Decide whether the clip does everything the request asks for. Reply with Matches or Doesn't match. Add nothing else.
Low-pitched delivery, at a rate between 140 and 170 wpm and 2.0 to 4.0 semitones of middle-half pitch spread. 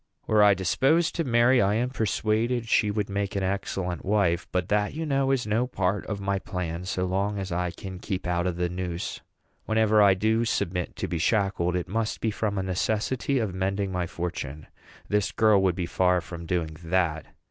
Doesn't match